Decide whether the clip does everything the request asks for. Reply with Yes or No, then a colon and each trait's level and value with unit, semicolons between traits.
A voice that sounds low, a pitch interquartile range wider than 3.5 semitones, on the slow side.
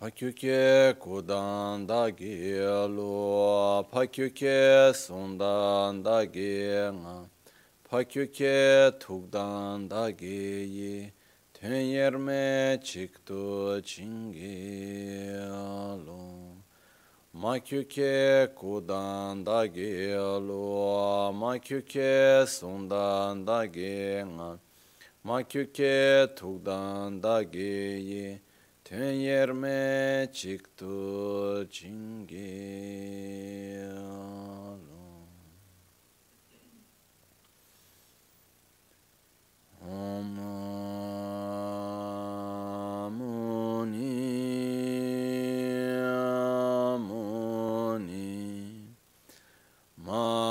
Yes: low, 100 Hz; average, 4.0 semitones; slow, 35 wpm